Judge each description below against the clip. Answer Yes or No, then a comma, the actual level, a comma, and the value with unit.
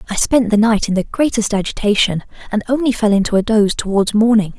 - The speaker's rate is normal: No, fast, 210 wpm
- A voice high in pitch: Yes, high, 215 Hz